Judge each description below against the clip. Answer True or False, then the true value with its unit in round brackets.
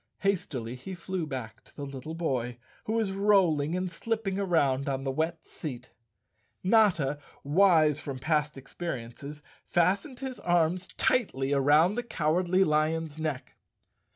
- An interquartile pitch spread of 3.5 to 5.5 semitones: True (5.2 semitones)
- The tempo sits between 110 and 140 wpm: True (135 wpm)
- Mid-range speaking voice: True (160 Hz)